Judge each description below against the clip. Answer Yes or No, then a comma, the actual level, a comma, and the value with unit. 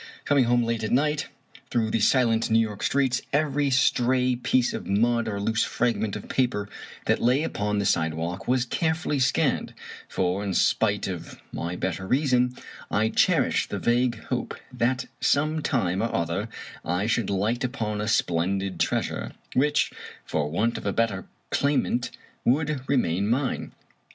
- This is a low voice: Yes, low, 115 Hz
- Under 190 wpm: Yes, average, 160 wpm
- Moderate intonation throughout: Yes, average, 4.3 semitones